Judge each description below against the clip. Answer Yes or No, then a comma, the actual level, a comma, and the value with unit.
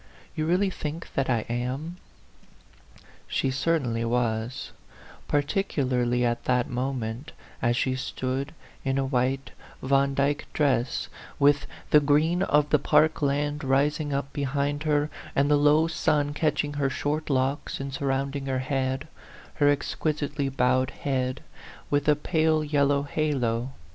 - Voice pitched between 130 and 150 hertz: Yes, medium, 140 Hz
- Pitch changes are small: Yes, narrow, 2.2 semitones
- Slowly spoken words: No, average, 145 wpm